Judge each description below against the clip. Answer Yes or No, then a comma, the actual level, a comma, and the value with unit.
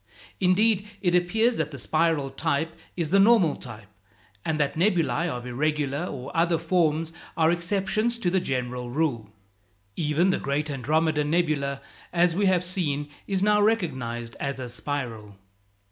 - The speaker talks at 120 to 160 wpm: Yes, average, 150 wpm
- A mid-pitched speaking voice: Yes, medium, 160 Hz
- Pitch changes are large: No, average, 4.5 semitones